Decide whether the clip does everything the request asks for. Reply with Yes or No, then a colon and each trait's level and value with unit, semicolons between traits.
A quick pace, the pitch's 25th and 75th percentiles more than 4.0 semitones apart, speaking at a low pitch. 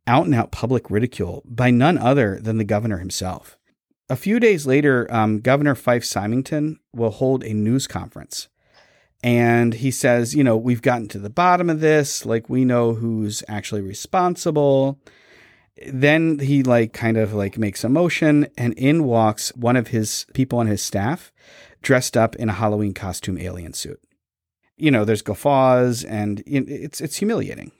No: average, 170 wpm; average, 4.4 semitones; low, 120 Hz